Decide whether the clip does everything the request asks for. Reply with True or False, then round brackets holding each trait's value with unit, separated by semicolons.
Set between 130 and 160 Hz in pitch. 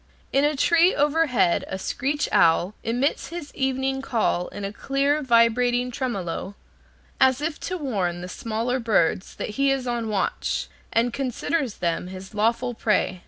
False (245 Hz)